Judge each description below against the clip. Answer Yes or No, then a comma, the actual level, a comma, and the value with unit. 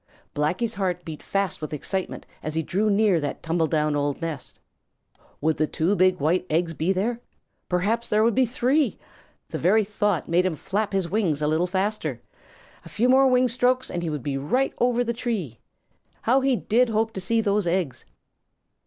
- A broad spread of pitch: Yes, wide, 5.8 semitones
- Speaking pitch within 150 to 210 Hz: Yes, high, 190 Hz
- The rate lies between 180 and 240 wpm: Yes, average, 190 wpm